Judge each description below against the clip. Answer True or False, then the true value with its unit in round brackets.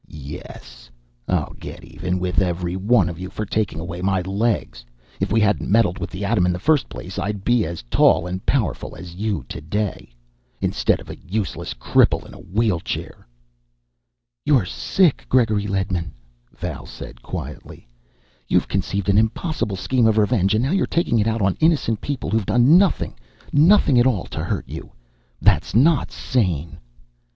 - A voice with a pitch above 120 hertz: False (100 Hz)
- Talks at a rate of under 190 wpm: True (165 wpm)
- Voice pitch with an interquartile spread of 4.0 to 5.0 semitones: True (4.7 semitones)